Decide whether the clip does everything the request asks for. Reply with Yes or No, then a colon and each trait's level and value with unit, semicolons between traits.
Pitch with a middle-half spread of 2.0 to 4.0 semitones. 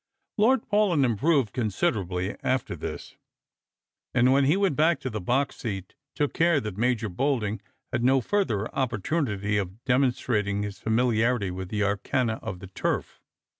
No: average, 5.1 semitones